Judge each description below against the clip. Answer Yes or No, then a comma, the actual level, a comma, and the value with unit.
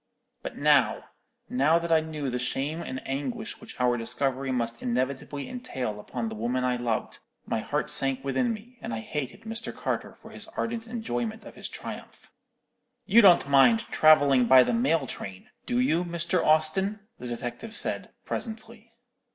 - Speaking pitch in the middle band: Yes, medium, 145 Hz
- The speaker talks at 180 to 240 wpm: No, average, 165 wpm